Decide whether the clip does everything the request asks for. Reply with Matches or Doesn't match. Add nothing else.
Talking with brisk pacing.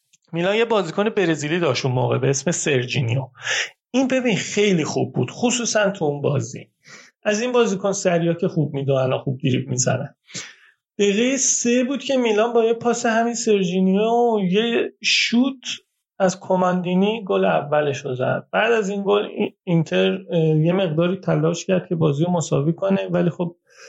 Matches